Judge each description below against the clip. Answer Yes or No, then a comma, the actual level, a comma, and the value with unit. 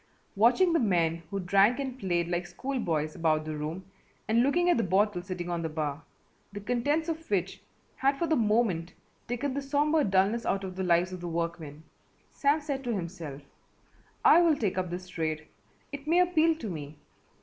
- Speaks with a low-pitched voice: No, high, 195 Hz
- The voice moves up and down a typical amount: No, wide, 8.2 semitones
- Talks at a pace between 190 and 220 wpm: Yes, average, 195 wpm